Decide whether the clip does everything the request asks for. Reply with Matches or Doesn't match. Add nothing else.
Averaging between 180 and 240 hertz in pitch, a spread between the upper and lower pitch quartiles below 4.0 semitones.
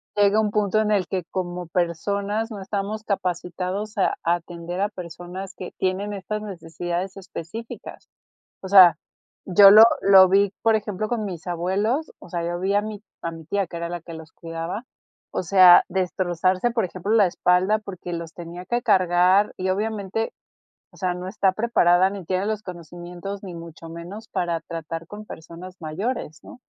Matches